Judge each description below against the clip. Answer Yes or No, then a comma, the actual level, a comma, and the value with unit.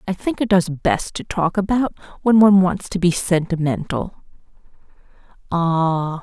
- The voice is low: No, medium, 180 Hz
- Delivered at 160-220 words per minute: No, slow, 135 wpm